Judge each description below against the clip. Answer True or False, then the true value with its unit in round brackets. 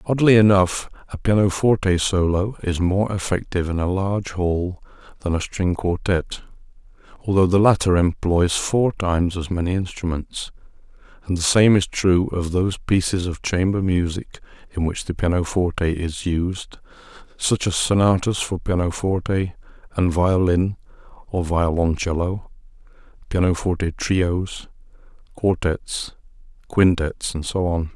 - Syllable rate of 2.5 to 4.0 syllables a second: False (4.5 syllables/s)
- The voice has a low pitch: True (90 Hz)